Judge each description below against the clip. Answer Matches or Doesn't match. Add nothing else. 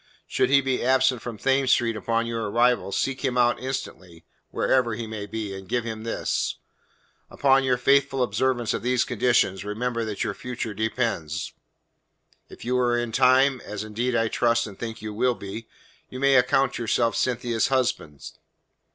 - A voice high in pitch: Doesn't match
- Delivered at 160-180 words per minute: Matches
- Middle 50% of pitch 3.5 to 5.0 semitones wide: Doesn't match